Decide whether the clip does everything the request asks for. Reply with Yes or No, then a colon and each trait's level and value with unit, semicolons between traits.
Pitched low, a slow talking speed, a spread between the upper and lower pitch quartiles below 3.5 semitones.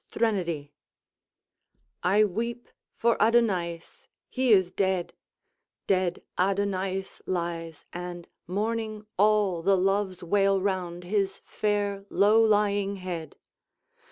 No: high, 195 Hz; slow, 100 wpm; average, 2.7 semitones